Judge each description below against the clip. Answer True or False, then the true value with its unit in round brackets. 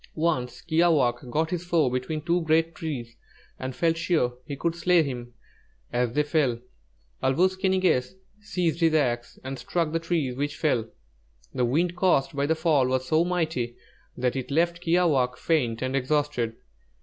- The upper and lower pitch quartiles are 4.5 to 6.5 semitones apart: True (4.8 semitones)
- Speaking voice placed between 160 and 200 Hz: False (150 Hz)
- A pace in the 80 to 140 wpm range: False (175 wpm)